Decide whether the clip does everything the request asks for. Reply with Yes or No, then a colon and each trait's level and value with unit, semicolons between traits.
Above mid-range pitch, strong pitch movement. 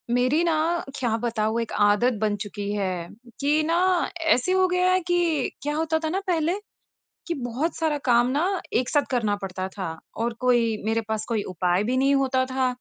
Yes: very high, 250 Hz; wide, 6.1 semitones